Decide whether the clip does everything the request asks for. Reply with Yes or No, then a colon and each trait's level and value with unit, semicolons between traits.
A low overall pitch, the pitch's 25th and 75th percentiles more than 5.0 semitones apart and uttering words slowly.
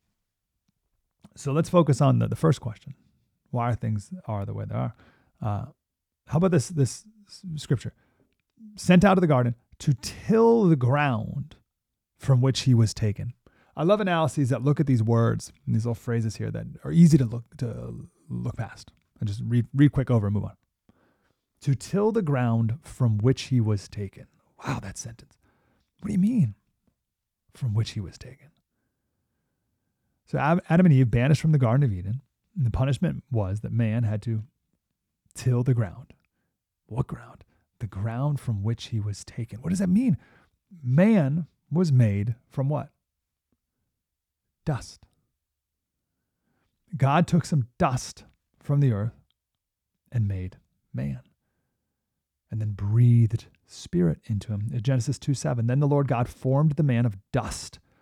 No: low, 125 Hz; wide, 5.4 semitones; average, 160 wpm